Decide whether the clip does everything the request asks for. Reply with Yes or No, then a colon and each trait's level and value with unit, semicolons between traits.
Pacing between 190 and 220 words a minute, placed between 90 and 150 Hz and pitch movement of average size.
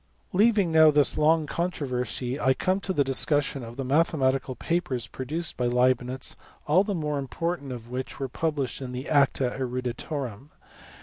No: average, 160 wpm; medium, 140 Hz; average, 4.0 semitones